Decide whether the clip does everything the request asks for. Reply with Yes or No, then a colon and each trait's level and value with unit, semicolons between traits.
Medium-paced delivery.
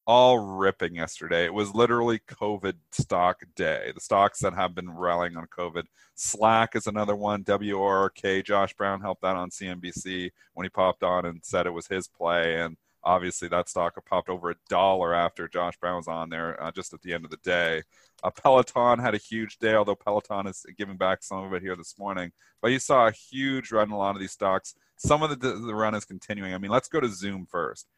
No: fast, 220 wpm